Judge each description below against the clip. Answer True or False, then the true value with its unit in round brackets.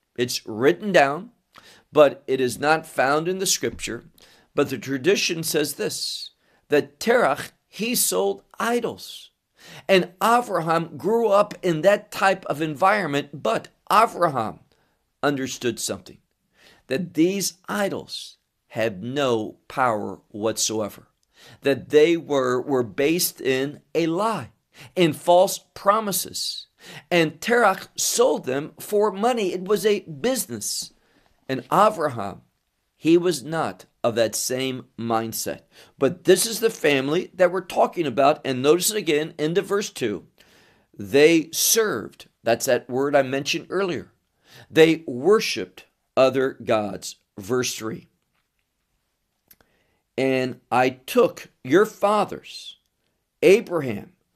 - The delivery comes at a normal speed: False (120 wpm)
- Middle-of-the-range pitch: True (160 Hz)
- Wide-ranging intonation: True (6.8 semitones)